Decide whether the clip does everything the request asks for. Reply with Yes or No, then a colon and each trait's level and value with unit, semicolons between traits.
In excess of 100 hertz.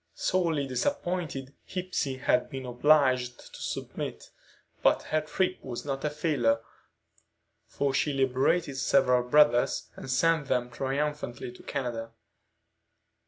Yes: low, 135 Hz